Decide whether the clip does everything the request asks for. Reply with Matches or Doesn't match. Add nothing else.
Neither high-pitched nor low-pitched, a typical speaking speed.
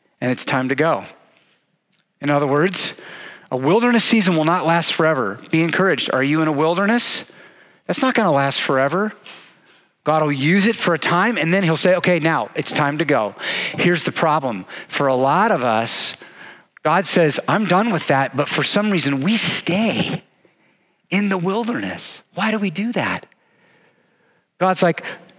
Matches